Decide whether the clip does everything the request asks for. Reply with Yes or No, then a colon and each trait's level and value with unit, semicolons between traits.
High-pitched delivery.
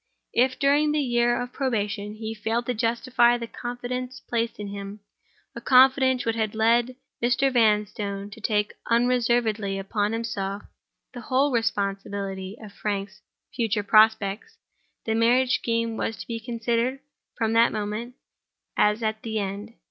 Yes: high, 230 Hz